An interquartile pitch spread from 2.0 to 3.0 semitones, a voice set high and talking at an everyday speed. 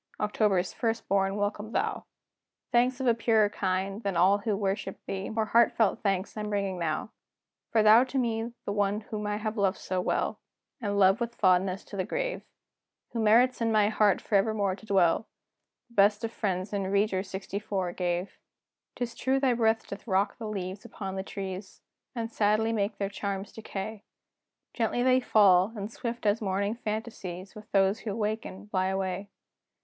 Yes: narrow, 2.5 semitones; high, 205 Hz; average, 175 wpm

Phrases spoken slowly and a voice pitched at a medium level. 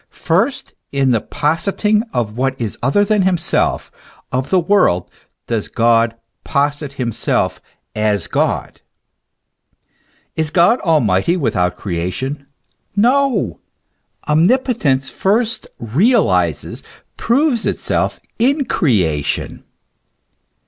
Yes: slow, 95 wpm; medium, 145 Hz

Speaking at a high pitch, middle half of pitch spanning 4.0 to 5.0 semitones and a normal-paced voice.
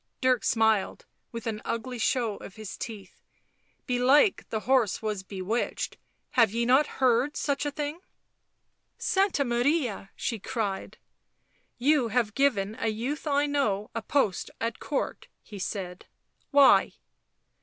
Yes: high, 235 Hz; average, 4.5 semitones; average, 155 wpm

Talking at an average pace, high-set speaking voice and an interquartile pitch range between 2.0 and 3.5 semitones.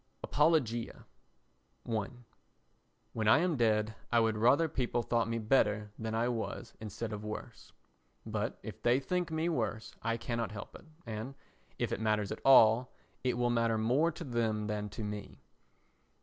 No: average, 165 wpm; low, 115 Hz; narrow, 2.5 semitones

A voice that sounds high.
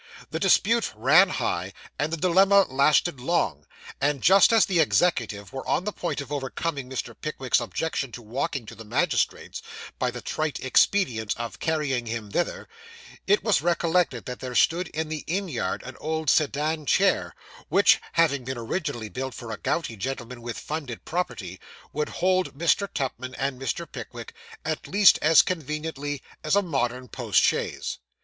No: medium, 145 Hz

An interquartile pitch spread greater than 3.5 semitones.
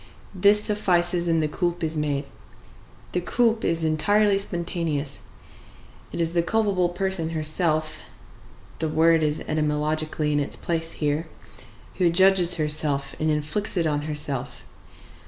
No: average, 2.7 semitones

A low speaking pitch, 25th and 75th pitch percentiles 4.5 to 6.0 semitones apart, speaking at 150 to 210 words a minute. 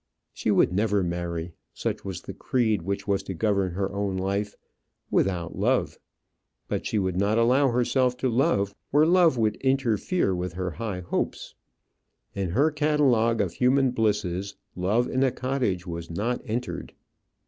Yes: low, 105 Hz; average, 5.1 semitones; average, 160 wpm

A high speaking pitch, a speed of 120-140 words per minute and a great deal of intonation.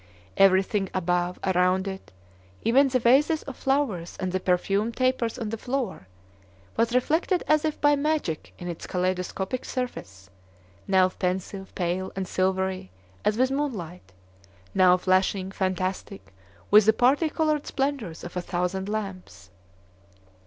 Yes: high, 195 Hz; slow, 135 wpm; wide, 5.8 semitones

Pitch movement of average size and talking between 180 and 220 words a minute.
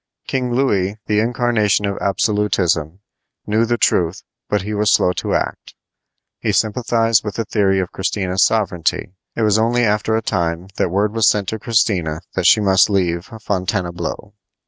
No: average, 3.1 semitones; average, 165 wpm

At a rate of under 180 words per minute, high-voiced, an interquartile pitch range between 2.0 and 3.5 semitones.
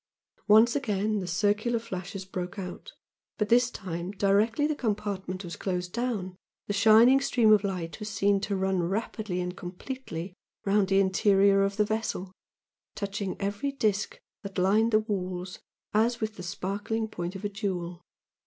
Yes: average, 160 wpm; high, 200 Hz; average, 2.7 semitones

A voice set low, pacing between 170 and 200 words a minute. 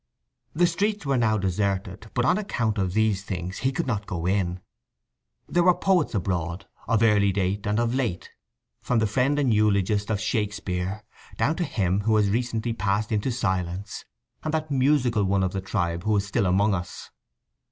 Yes: low, 105 Hz; average, 185 wpm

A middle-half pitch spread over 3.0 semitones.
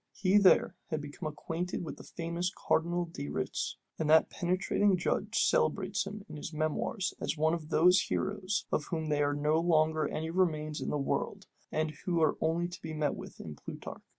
No: average, 2.7 semitones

